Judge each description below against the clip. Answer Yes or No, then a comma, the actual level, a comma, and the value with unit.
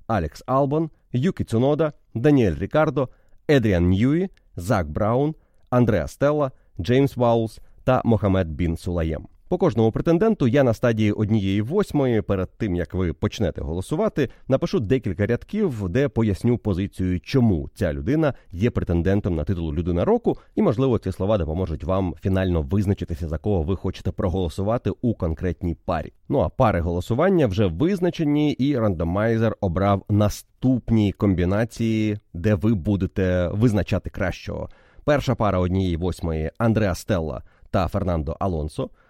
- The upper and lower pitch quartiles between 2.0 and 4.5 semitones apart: No, average, 5.3 semitones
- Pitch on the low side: Yes, low, 105 Hz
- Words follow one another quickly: No, average, 135 wpm